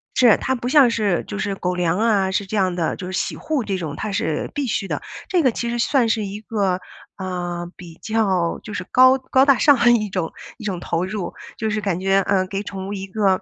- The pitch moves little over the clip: No, average, 3.6 semitones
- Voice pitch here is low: No, high, 200 Hz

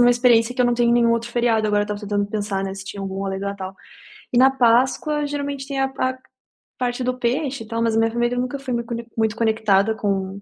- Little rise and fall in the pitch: No, average, 3.3 semitones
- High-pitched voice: Yes, high, 235 Hz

